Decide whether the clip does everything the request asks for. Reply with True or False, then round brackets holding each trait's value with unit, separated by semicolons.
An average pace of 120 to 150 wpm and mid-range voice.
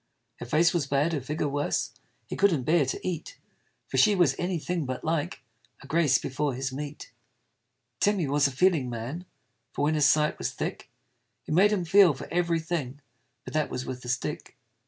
False (200 wpm; 150 Hz)